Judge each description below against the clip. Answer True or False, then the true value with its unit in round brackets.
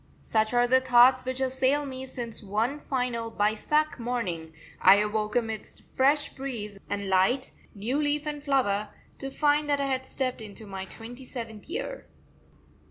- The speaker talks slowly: False (160 wpm)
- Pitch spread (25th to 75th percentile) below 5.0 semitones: True (4.2 semitones)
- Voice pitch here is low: False (245 Hz)